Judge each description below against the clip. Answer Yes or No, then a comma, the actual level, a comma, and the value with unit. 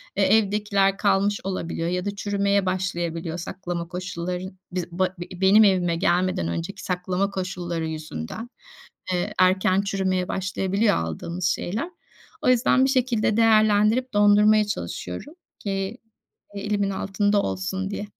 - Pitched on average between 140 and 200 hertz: Yes, high, 190 Hz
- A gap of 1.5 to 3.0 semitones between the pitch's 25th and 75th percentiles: Yes, narrow, 2.4 semitones